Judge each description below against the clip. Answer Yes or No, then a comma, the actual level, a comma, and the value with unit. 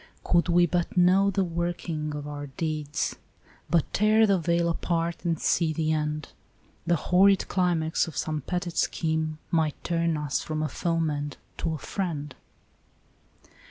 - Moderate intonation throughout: No, narrow, 2.3 semitones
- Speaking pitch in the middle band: Yes, medium, 165 Hz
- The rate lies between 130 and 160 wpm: Yes, average, 155 wpm